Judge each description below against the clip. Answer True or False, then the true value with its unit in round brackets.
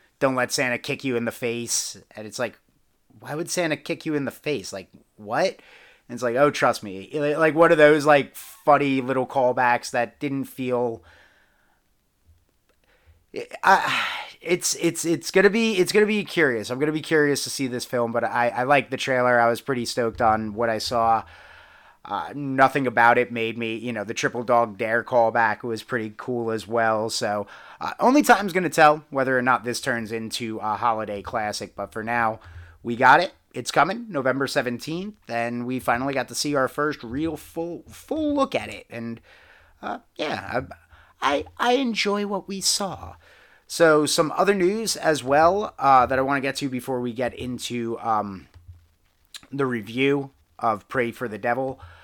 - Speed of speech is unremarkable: True (185 wpm)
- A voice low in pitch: True (125 Hz)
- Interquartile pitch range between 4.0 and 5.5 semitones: True (4.5 semitones)